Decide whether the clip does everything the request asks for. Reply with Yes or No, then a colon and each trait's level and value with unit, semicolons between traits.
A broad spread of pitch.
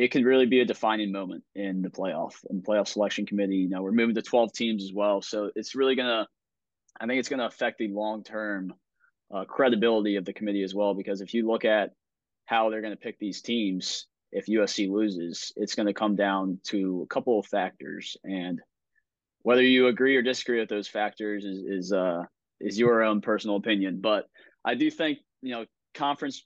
No: average, 2.9 semitones